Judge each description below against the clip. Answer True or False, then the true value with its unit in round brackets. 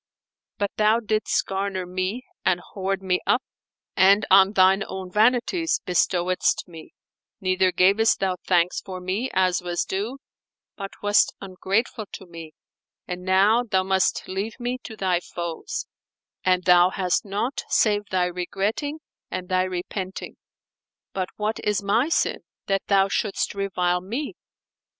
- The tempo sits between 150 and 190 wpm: False (140 wpm)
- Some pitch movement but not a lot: False (2.3 semitones)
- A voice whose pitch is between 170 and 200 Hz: True (190 Hz)